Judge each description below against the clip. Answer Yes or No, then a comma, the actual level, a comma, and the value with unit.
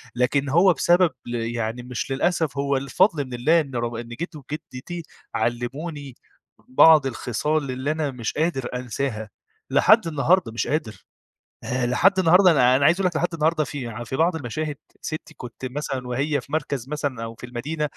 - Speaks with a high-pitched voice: No, medium, 140 Hz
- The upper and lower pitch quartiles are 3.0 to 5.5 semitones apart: Yes, average, 4.4 semitones